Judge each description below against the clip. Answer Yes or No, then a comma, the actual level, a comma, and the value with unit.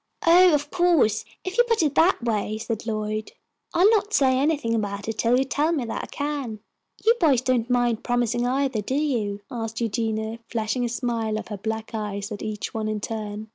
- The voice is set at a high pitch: Yes, high, 235 Hz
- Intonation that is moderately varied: Yes, average, 4.5 semitones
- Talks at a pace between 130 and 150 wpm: No, fast, 205 wpm